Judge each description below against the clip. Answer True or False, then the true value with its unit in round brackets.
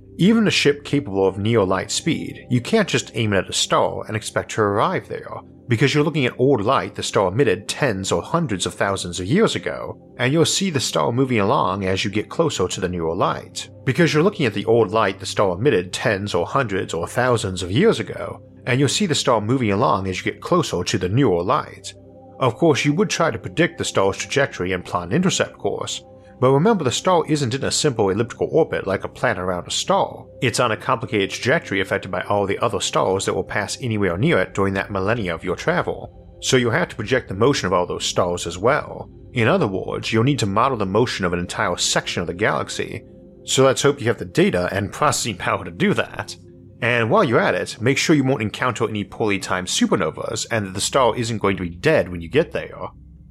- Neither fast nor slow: False (235 wpm)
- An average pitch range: False (5.9 semitones)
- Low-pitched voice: True (110 Hz)